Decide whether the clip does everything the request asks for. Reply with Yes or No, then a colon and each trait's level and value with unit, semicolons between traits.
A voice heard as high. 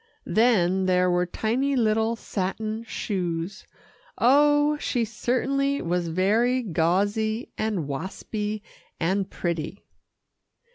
Yes: high, 215 Hz